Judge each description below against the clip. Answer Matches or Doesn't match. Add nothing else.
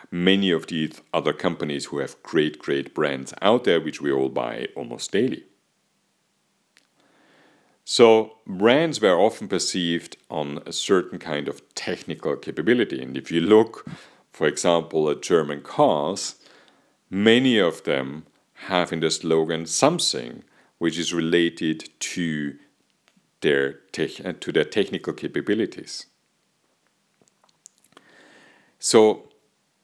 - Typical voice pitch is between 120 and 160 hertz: Doesn't match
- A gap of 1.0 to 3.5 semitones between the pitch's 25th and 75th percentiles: Matches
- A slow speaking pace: Matches